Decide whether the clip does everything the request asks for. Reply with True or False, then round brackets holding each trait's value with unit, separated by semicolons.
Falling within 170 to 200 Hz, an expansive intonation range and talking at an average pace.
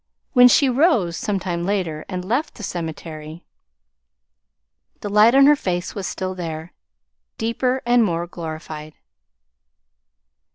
False (185 Hz; 6.0 semitones; 120 wpm)